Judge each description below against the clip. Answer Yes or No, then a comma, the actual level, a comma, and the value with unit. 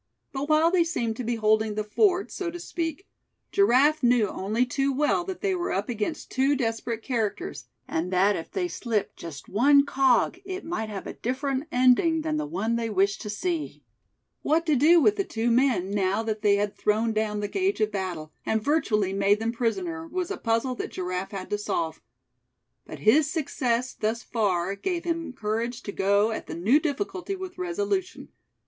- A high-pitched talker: Yes, high, 245 Hz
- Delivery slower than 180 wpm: No, average, 190 wpm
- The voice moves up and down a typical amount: No, wide, 7.4 semitones